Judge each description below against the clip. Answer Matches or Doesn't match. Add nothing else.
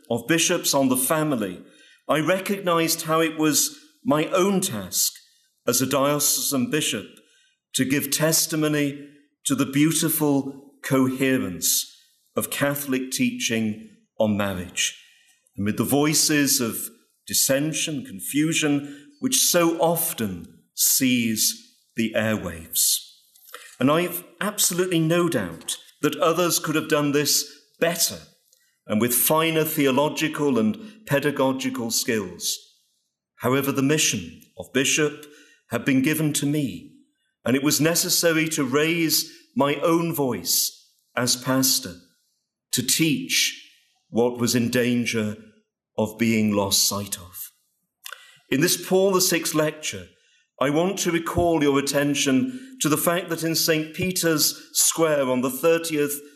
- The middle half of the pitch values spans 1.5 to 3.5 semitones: Doesn't match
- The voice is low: Doesn't match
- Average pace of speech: Doesn't match